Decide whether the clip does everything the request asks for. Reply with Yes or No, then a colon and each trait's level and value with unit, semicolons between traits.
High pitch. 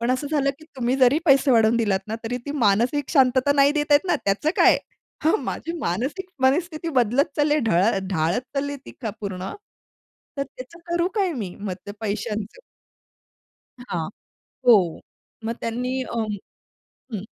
Yes: very high, 255 Hz